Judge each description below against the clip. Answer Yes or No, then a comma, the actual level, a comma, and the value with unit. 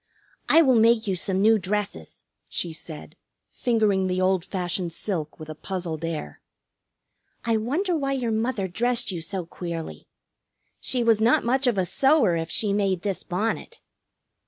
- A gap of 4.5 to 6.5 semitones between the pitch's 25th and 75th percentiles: Yes, average, 5.0 semitones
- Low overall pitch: No, high, 200 Hz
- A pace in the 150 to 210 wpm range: Yes, average, 160 wpm